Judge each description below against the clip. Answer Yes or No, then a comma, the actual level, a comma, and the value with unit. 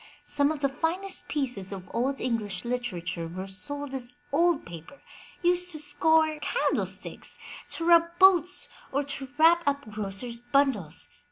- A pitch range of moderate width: No, wide, 7.1 semitones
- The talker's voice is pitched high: Yes, very high, 275 Hz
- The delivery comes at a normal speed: Yes, average, 145 wpm